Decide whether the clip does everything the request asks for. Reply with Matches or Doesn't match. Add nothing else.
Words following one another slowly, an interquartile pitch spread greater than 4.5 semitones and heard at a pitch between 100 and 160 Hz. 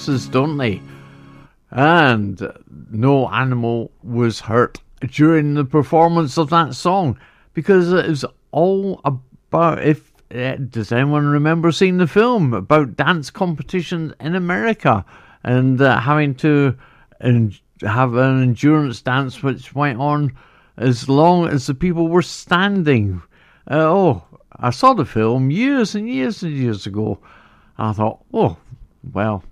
Matches